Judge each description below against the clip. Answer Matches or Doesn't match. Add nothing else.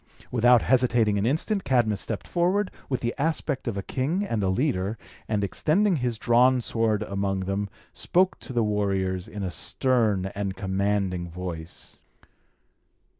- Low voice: Matches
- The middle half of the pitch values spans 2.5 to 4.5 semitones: Doesn't match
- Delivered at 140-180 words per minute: Matches